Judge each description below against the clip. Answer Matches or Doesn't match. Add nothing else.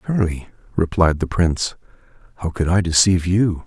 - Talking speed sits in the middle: Matches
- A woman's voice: Doesn't match